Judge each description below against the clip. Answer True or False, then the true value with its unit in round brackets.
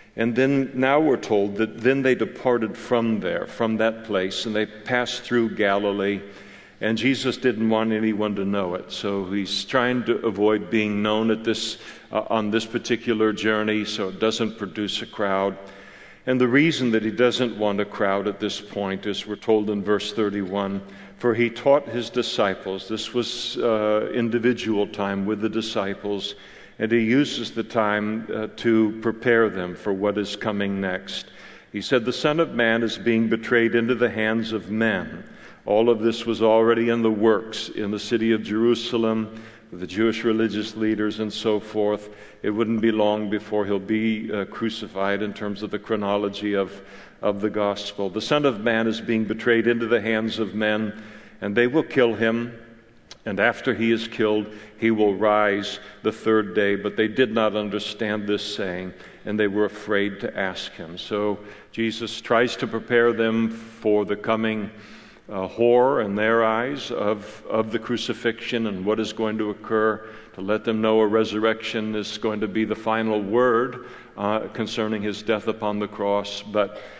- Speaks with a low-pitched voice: True (110 Hz)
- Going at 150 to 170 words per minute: False (180 wpm)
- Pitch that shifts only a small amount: True (1.7 semitones)